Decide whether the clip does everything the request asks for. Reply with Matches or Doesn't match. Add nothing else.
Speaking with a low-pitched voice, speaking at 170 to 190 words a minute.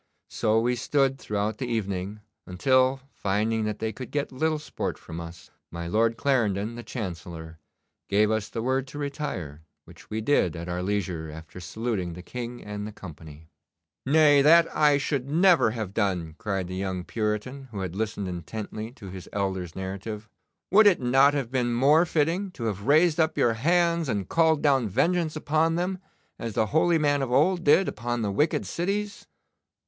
Matches